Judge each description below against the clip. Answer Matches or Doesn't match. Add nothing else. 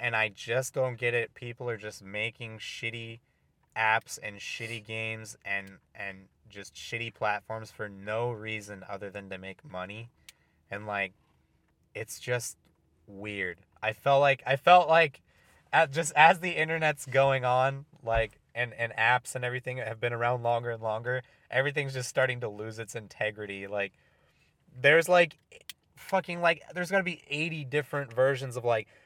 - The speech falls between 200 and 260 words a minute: Doesn't match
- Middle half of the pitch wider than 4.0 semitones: Matches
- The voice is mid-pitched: Doesn't match